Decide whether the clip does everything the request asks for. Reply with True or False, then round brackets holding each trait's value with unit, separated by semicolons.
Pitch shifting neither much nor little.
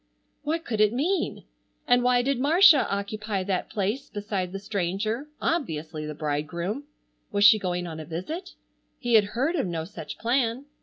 False (6.2 semitones)